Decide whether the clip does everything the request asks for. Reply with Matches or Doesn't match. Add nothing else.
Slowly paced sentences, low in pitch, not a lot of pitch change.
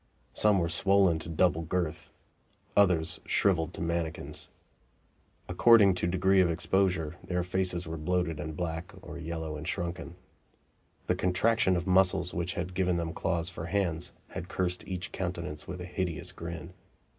Doesn't match